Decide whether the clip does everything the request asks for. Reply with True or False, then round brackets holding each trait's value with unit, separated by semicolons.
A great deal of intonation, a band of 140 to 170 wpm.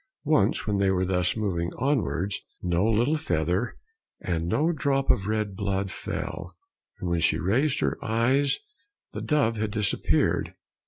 True (6.1 semitones; 150 wpm)